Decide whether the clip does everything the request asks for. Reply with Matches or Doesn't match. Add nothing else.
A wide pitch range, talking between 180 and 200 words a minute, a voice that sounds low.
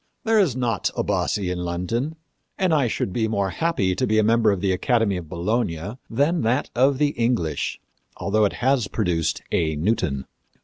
Matches